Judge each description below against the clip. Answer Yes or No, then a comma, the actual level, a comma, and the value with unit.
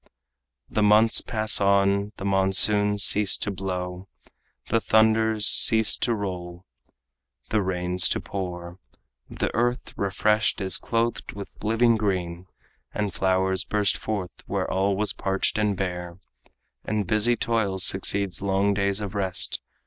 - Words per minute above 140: No, slow, 135 wpm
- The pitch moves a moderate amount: No, narrow, 2.2 semitones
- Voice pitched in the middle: No, low, 100 Hz